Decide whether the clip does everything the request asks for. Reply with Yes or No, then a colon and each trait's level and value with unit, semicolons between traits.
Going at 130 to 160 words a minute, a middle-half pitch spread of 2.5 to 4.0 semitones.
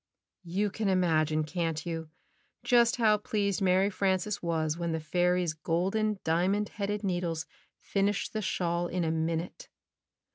Yes: average, 140 wpm; average, 3.7 semitones